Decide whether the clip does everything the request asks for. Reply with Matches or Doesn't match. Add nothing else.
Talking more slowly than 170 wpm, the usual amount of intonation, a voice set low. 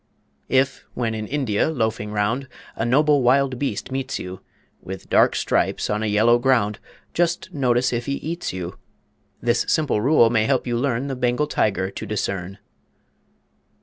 Matches